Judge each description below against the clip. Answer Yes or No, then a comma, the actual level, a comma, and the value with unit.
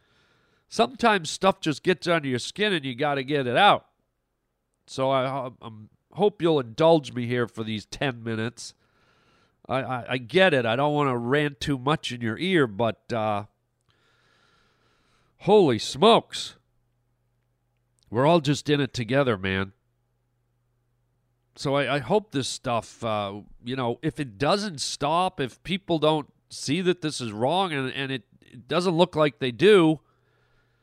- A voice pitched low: Yes, low, 130 Hz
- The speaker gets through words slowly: No, average, 160 wpm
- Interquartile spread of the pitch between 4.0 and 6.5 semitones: Yes, average, 4.3 semitones